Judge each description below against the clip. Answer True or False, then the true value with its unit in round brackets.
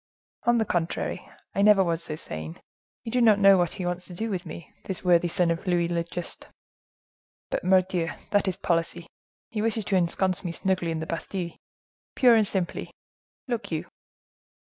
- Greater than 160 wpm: True (175 wpm)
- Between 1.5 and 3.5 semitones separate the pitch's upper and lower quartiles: True (2.9 semitones)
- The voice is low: False (180 Hz)